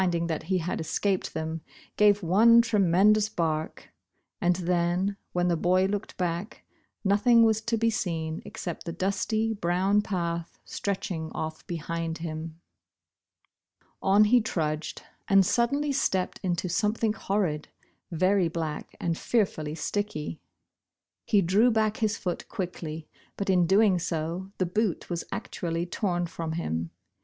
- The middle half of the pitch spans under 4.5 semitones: Yes, average, 3.8 semitones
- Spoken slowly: No, average, 145 wpm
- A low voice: No, medium, 180 Hz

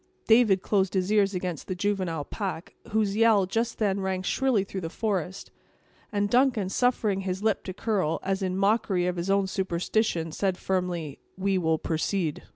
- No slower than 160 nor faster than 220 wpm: Yes, average, 170 wpm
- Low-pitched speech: No, high, 190 Hz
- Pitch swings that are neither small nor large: No, narrow, 2.3 semitones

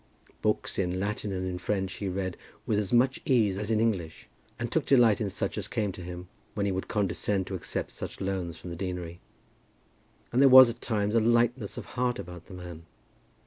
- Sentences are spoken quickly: Yes, fast, 210 wpm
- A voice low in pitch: Yes, low, 100 Hz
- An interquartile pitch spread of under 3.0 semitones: No, average, 3.8 semitones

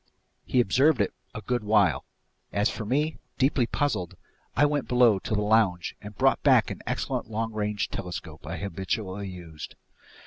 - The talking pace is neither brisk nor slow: Yes, average, 165 wpm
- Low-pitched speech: Yes, low, 105 Hz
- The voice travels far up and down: No, average, 4.5 semitones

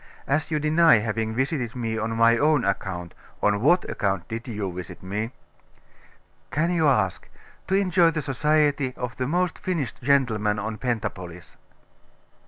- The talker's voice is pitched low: Yes, low, 120 Hz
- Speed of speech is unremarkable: Yes, average, 150 wpm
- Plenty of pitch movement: Yes, wide, 6.2 semitones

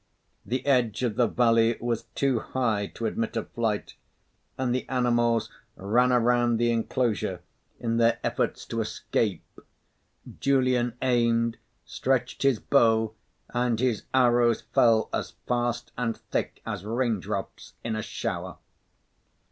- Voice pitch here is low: Yes, low, 120 Hz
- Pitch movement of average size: No, narrow, 1.5 semitones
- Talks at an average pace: No, slow, 130 wpm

